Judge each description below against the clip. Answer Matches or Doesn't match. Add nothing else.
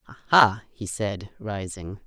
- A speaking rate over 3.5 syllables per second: Doesn't match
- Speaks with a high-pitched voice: Doesn't match